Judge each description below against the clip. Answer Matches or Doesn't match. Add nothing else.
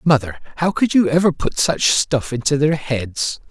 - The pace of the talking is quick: Doesn't match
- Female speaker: Doesn't match